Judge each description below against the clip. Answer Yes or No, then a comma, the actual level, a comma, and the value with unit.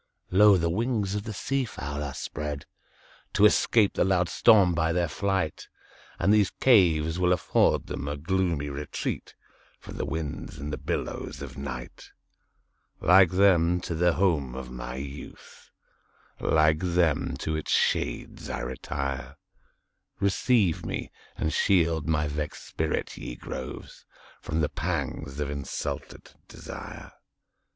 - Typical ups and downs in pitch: Yes, average, 4.5 semitones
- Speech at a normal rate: No, slow, 125 wpm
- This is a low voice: Yes, very low, 80 Hz